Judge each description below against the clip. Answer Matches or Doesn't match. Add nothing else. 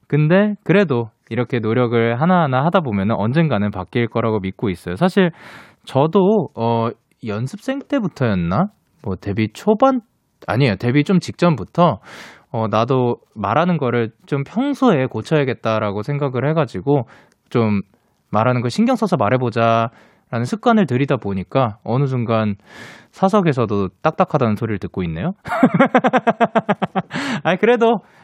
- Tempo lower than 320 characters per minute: Matches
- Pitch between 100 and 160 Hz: Matches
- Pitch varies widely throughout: Matches